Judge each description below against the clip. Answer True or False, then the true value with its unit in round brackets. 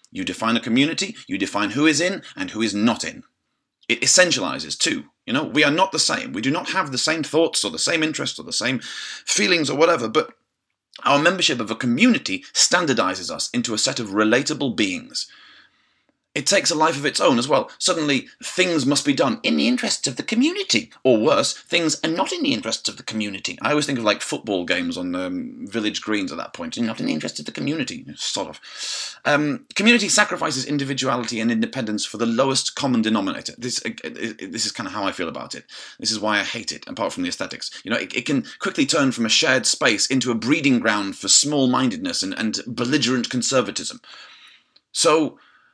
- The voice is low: False (160 Hz)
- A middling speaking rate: False (215 wpm)